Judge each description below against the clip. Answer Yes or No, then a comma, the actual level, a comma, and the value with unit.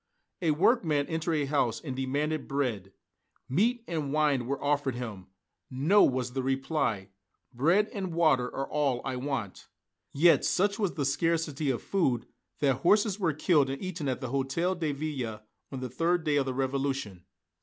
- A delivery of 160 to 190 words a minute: Yes, average, 170 wpm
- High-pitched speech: No, medium, 140 Hz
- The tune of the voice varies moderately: Yes, average, 4.0 semitones